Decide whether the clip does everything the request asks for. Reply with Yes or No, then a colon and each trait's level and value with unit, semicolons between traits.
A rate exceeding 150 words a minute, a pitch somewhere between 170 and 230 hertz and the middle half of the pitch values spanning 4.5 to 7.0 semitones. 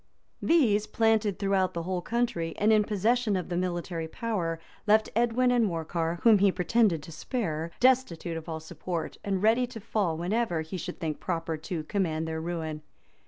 Yes: average, 180 wpm; medium, 185 Hz; average, 5.1 semitones